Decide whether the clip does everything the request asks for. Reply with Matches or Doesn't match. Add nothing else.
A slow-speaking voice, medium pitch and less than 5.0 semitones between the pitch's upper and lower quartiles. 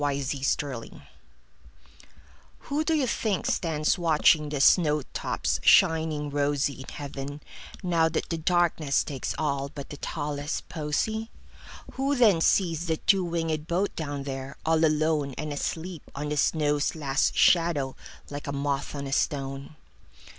Matches